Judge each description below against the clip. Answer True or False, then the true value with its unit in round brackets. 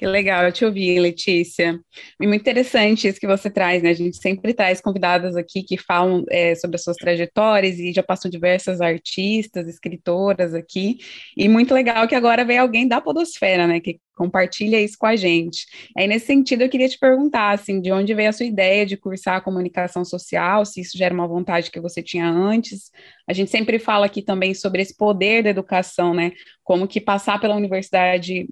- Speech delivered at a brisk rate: True (200 wpm)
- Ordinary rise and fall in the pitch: True (3.2 semitones)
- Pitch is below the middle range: False (190 Hz)